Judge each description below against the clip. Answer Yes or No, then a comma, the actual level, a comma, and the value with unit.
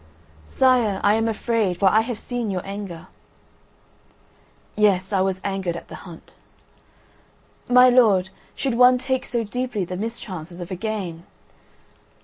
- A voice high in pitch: Yes, high, 205 Hz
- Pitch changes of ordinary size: Yes, average, 4.3 semitones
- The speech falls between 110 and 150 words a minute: Yes, average, 140 wpm